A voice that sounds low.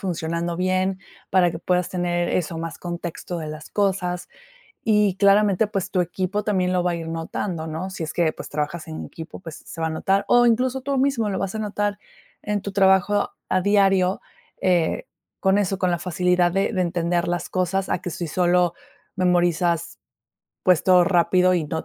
No: medium, 180 Hz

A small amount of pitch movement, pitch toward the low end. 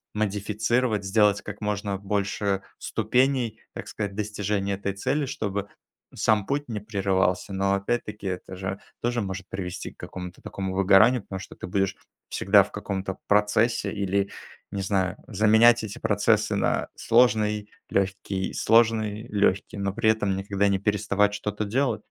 Yes: narrow, 1.8 semitones; low, 100 Hz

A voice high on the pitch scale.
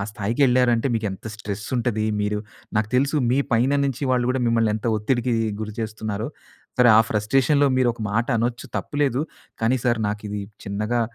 No: low, 115 Hz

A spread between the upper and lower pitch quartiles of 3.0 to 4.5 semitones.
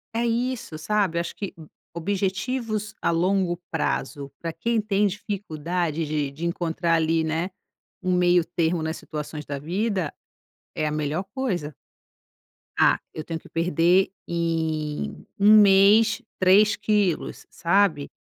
Yes: average, 4.0 semitones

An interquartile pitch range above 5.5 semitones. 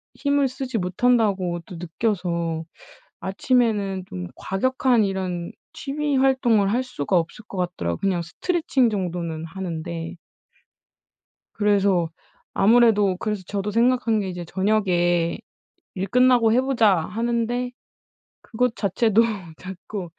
No: average, 5.2 semitones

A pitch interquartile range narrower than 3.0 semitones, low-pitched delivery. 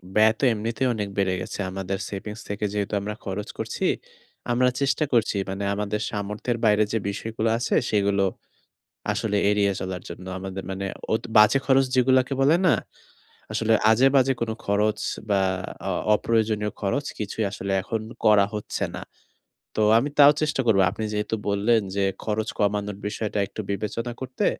Yes: narrow, 2.5 semitones; low, 105 Hz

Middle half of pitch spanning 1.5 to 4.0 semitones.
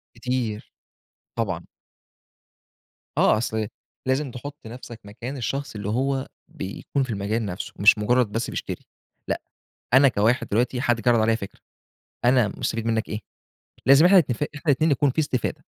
Yes: average, 3.5 semitones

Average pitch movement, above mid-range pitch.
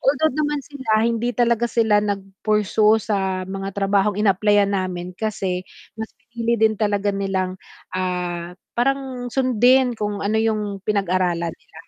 Yes: average, 3.3 semitones; high, 210 Hz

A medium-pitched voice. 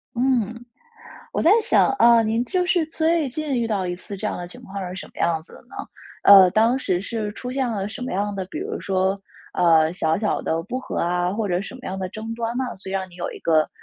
No: high, 205 Hz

